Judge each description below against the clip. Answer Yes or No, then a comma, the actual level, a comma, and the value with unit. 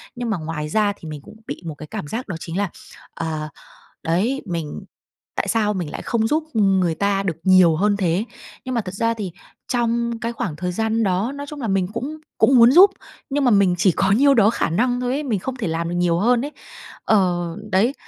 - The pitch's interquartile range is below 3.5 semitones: No, average, 5.2 semitones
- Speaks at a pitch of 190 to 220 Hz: Yes, high, 205 Hz